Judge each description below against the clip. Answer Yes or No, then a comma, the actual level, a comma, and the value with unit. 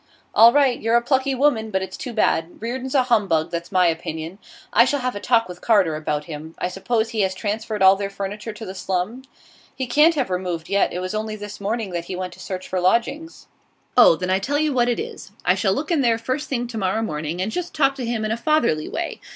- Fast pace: Yes, fast, 250 wpm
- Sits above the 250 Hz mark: No, high, 215 Hz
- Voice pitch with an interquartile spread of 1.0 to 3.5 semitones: No, average, 4.8 semitones